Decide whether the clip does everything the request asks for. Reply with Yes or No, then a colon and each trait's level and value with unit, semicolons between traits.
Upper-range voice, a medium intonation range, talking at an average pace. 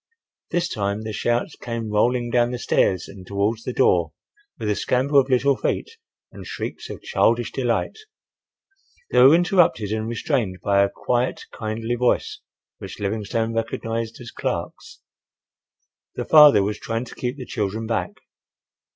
No: low, 115 Hz; average, 3.0 semitones; average, 150 wpm